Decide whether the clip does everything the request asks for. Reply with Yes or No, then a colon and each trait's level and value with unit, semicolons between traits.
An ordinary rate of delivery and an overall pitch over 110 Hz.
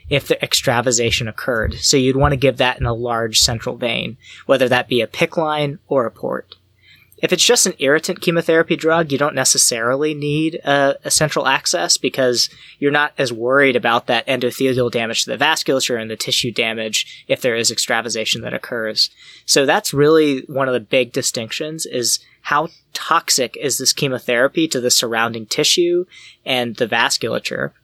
Yes: average, 175 wpm; low, 135 Hz